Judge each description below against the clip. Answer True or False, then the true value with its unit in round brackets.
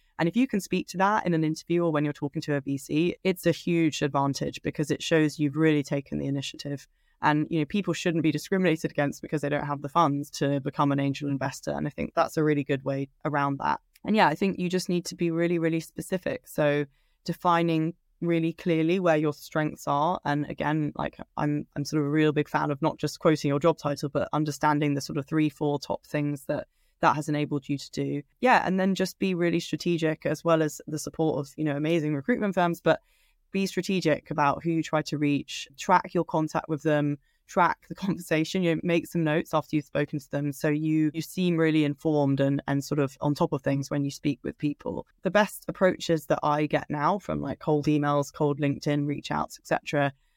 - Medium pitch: True (155 Hz)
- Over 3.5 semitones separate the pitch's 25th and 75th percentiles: False (2.5 semitones)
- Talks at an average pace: False (230 wpm)